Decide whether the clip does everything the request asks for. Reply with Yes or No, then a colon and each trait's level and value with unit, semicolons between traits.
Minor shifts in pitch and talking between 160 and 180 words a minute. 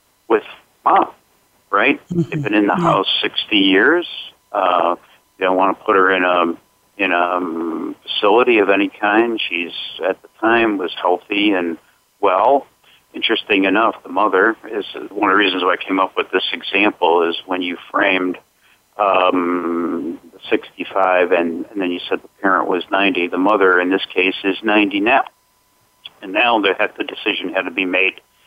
Yes: narrow, 1.9 semitones; average, 175 wpm